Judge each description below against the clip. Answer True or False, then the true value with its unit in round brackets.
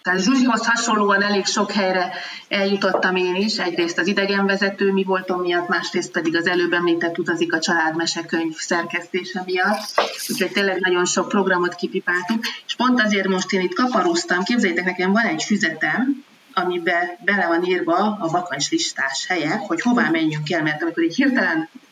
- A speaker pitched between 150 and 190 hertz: True (185 Hz)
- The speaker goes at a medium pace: False (160 wpm)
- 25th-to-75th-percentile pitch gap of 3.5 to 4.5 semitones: False (3.1 semitones)